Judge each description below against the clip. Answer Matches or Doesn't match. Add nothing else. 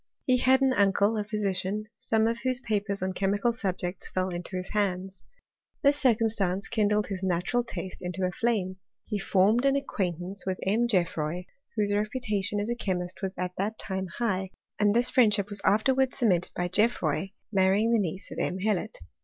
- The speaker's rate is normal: Matches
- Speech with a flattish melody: Doesn't match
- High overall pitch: Matches